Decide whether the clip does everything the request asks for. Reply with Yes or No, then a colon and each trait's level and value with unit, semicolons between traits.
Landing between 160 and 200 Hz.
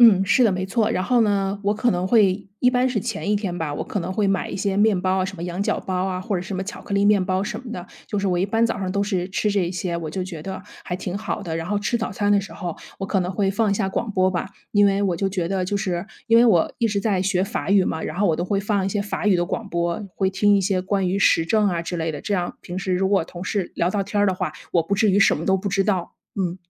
Yes: high, 195 Hz